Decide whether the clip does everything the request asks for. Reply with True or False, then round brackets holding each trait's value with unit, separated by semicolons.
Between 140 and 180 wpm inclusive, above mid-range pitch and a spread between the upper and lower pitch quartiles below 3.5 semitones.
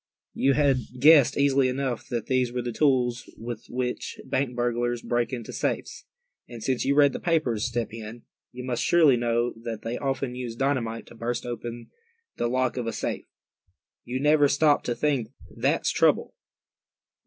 False (175 wpm; 125 Hz; 2.4 semitones)